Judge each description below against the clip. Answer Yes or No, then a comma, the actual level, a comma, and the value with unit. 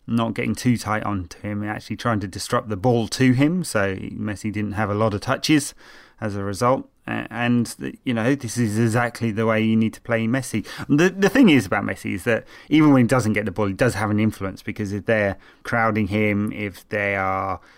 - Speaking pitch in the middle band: No, low, 110 Hz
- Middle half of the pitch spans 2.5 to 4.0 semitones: Yes, average, 2.8 semitones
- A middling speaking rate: No, fast, 225 wpm